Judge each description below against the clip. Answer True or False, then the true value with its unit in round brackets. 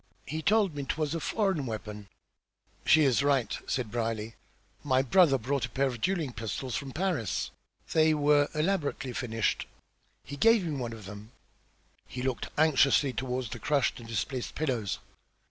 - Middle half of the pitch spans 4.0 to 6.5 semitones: True (4.9 semitones)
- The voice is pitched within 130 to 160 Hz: True (135 Hz)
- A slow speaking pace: False (160 wpm)